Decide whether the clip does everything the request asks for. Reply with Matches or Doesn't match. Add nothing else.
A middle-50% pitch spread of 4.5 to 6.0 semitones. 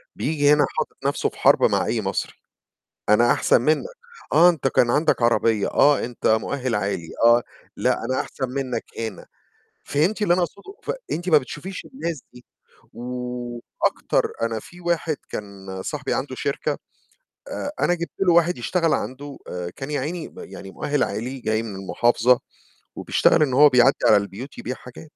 Matches